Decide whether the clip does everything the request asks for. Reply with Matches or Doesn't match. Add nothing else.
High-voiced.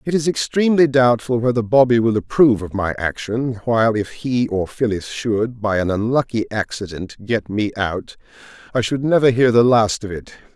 Doesn't match